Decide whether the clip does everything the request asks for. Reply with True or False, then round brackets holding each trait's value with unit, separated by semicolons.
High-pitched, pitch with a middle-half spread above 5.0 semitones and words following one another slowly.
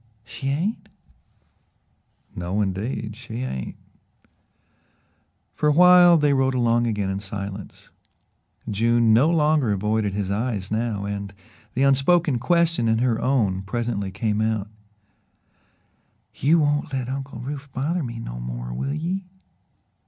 False (120 Hz; 5.6 semitones; 130 wpm)